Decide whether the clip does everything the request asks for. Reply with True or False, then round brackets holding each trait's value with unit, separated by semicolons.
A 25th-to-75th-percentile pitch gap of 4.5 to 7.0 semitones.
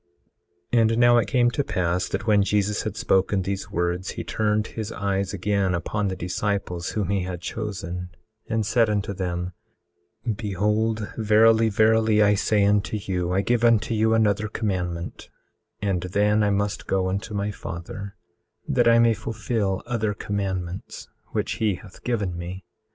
False (2.8 semitones)